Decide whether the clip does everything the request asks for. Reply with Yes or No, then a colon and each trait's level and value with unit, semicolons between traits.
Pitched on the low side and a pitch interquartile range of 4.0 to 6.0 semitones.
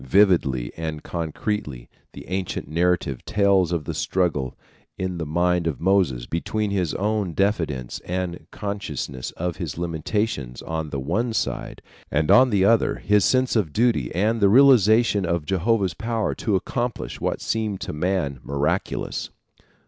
Yes: very low, 90 Hz; average, 5.0 semitones